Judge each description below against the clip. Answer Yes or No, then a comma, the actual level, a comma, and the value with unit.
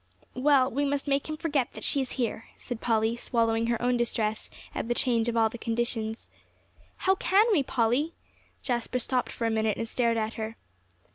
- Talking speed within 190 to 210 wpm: Yes, average, 195 wpm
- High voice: Yes, high, 240 Hz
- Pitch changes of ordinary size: Yes, average, 3.2 semitones